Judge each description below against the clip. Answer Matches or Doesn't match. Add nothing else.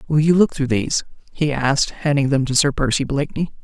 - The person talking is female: Matches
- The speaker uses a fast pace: Matches